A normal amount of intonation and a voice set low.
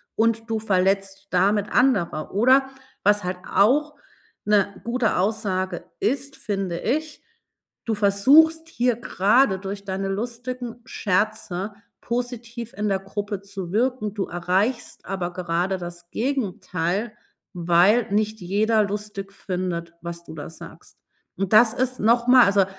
No: average, 3.9 semitones; high, 205 Hz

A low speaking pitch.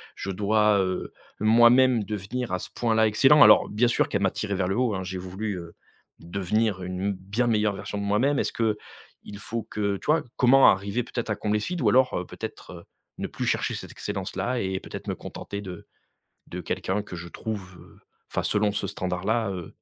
Yes: low, 105 Hz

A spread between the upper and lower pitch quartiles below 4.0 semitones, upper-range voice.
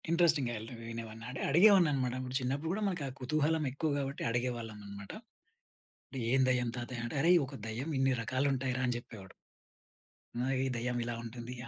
No: average, 3.3 semitones; low, 125 Hz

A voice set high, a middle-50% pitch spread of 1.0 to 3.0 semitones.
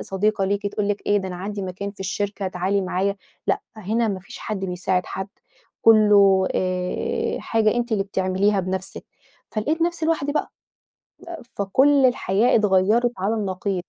Yes: high, 200 Hz; narrow, 2.6 semitones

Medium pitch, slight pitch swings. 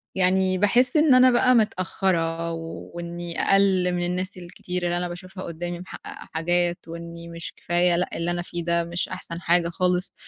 Yes: medium, 175 Hz; narrow, 1.5 semitones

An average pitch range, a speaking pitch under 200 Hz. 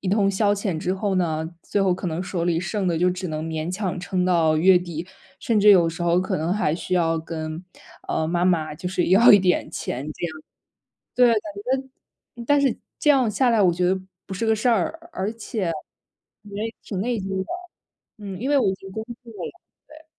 Yes: average, 3.7 semitones; high, 190 Hz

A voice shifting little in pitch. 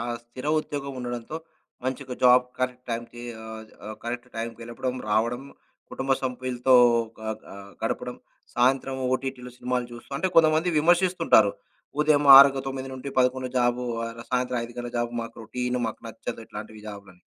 Yes: narrow, 2.1 semitones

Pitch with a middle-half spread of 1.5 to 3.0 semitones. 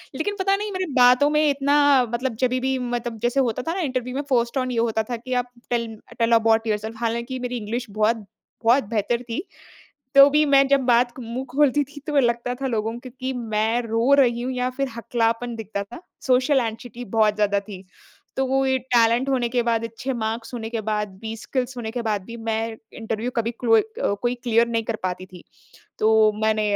Yes: narrow, 2.5 semitones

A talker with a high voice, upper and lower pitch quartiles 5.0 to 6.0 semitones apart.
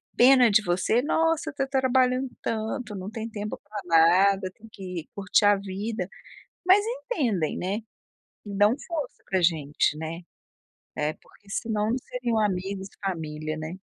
Yes: high, 205 Hz; average, 5.3 semitones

